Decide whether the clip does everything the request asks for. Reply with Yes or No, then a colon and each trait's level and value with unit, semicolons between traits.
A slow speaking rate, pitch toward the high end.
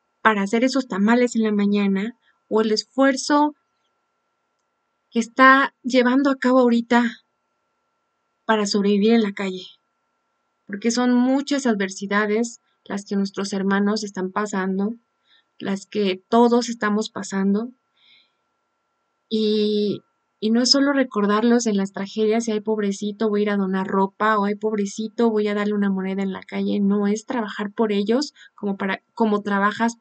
No: average, 150 wpm; high, 215 Hz